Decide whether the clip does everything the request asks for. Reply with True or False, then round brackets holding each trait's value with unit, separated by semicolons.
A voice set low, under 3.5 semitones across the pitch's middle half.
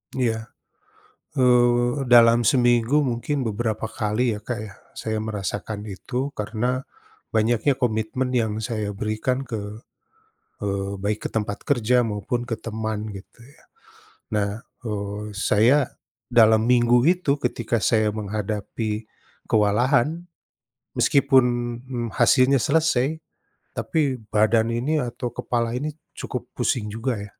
True (115 Hz; 2.8 semitones)